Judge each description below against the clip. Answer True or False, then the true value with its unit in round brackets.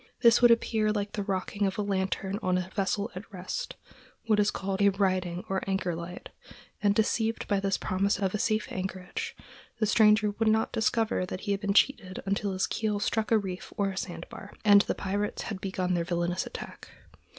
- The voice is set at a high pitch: True (200 Hz)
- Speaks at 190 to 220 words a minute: True (195 wpm)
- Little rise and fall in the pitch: True (2.2 semitones)